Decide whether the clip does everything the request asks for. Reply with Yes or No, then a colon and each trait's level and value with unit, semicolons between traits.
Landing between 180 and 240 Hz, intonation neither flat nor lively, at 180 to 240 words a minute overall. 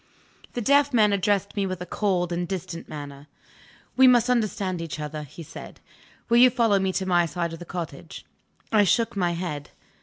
Yes: medium, 185 Hz; average, 4.1 semitones; average, 190 wpm